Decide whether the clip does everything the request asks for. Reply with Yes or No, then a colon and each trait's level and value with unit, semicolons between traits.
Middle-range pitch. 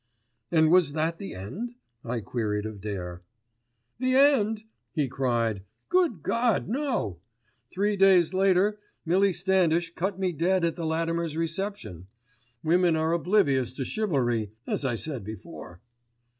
Yes: medium, 165 Hz